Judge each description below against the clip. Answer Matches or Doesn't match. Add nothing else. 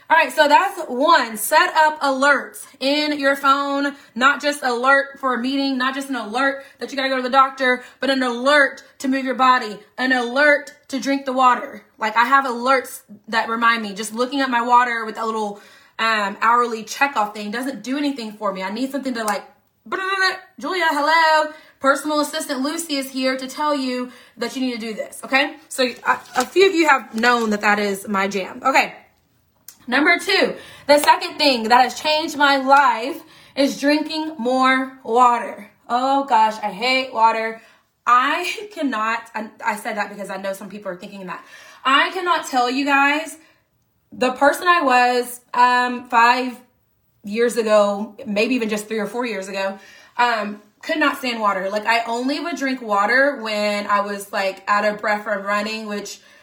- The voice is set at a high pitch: Matches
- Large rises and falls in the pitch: Doesn't match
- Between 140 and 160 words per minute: Doesn't match